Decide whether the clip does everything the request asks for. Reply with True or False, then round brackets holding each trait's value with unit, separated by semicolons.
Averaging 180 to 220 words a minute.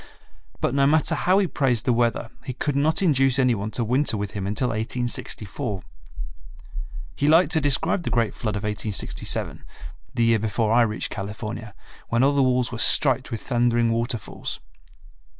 False (170 wpm)